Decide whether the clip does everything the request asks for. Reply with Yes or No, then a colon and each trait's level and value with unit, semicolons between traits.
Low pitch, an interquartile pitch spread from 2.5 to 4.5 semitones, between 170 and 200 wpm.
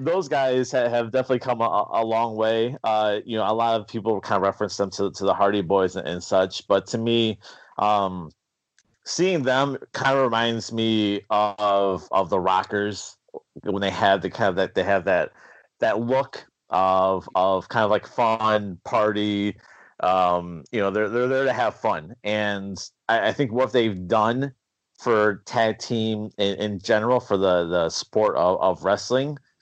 Yes: low, 110 Hz; average, 3.1 semitones; average, 180 wpm